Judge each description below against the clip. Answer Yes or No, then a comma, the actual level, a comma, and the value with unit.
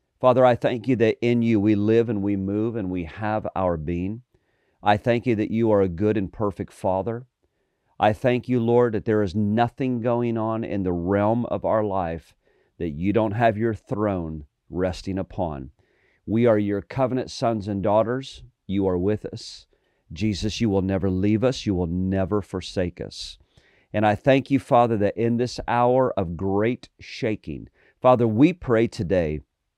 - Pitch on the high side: No, low, 105 Hz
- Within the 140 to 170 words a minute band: No, average, 180 wpm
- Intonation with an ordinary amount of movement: Yes, average, 3.7 semitones